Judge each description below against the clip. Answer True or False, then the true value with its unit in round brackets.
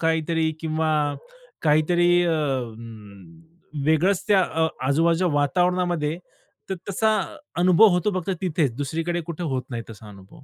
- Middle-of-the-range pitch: True (165 Hz)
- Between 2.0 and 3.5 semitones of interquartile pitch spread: True (2.8 semitones)